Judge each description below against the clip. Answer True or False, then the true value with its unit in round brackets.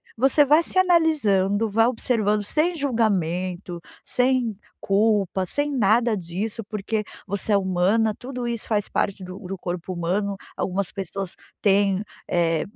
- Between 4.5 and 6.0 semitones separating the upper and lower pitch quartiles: False (4.0 semitones)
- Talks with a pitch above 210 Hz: False (205 Hz)